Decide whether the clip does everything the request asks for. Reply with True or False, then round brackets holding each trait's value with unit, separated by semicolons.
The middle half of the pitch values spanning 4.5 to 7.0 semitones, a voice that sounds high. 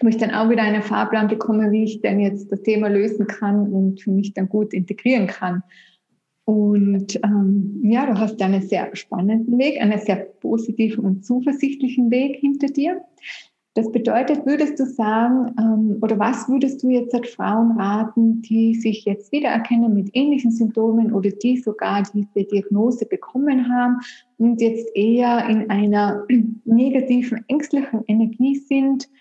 False (3.1 semitones; 225 Hz)